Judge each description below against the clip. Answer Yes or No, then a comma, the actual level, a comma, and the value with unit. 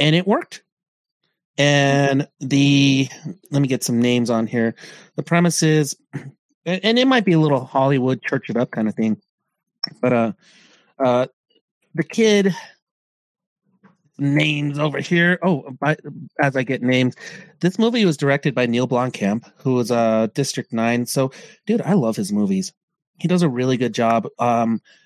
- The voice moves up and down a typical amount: No, wide, 5.7 semitones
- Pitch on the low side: No, medium, 145 Hz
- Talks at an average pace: Yes, average, 160 wpm